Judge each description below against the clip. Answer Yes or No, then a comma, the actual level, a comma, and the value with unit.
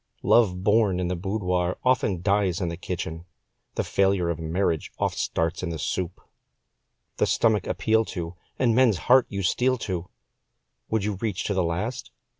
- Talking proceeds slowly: No, average, 170 wpm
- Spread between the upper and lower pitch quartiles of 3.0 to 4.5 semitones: Yes, average, 3.9 semitones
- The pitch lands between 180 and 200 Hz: No, very low, 95 Hz